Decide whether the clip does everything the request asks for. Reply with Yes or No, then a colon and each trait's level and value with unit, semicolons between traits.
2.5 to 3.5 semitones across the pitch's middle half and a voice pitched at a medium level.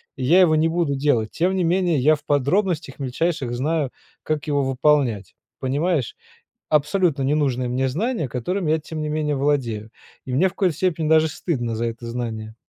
No: average, 4.2 semitones; medium, 150 Hz